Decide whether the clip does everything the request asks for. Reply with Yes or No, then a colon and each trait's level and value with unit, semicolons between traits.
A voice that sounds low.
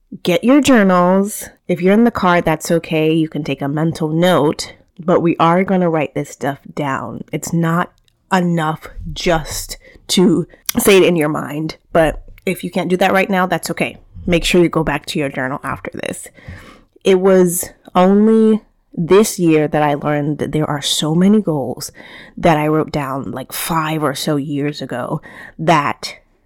No: medium, 165 Hz